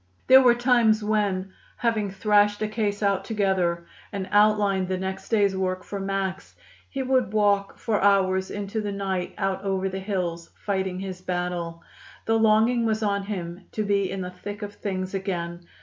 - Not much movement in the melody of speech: Yes, narrow, 2.1 semitones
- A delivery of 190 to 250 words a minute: No, average, 175 wpm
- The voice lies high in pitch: Yes, high, 195 Hz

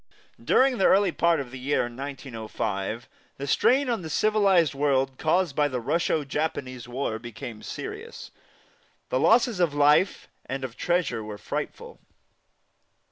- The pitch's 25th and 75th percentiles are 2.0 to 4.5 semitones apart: No, wide, 5.6 semitones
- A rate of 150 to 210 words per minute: No, average, 140 wpm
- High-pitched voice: No, medium, 140 Hz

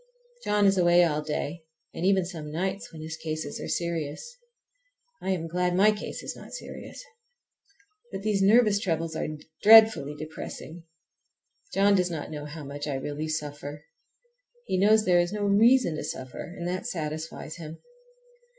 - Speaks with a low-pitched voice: No, medium, 170 Hz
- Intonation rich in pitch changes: No, average, 4.3 semitones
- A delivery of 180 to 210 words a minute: No, average, 160 wpm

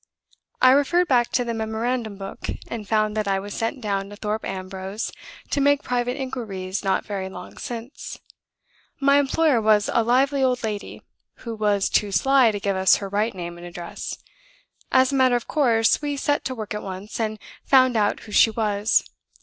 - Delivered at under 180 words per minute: No, average, 190 wpm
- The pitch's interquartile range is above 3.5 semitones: Yes, average, 4.1 semitones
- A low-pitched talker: No, high, 220 Hz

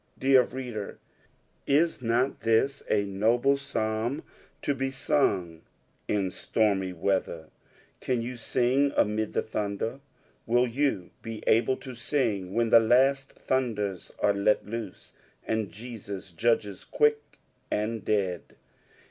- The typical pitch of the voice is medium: No, low, 115 Hz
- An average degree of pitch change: Yes, average, 4.2 semitones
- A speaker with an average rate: No, slow, 125 wpm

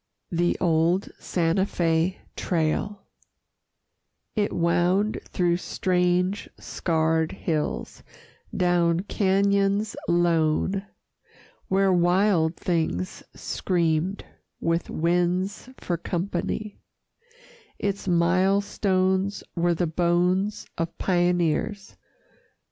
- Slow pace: Yes, slow, 80 wpm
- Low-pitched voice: No, medium, 180 Hz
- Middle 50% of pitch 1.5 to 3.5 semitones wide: Yes, narrow, 2.4 semitones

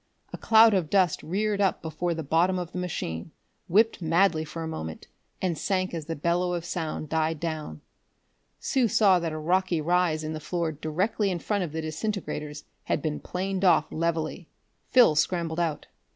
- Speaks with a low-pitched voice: No, medium, 170 Hz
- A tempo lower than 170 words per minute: No, average, 180 wpm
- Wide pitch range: No, average, 3.0 semitones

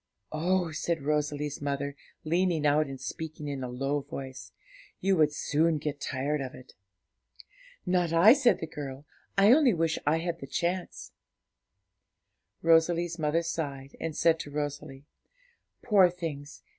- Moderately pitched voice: Yes, medium, 155 Hz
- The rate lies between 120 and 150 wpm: Yes, average, 145 wpm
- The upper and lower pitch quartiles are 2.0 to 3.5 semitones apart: Yes, average, 3.0 semitones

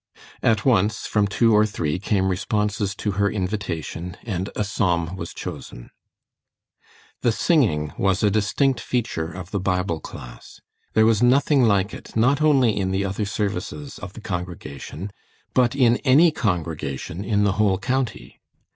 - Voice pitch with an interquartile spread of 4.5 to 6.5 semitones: No, average, 3.8 semitones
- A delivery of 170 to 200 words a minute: No, average, 155 wpm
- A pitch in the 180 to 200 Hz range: No, low, 100 Hz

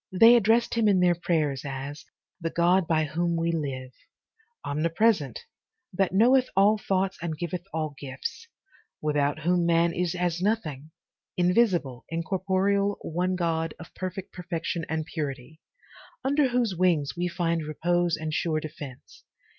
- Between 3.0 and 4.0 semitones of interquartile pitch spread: Yes, average, 3.4 semitones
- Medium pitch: Yes, medium, 170 Hz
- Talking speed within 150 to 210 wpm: No, average, 140 wpm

